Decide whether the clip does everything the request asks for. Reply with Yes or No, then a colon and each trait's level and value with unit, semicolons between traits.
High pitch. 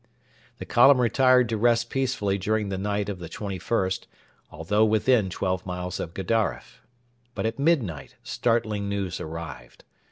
No: low, 105 Hz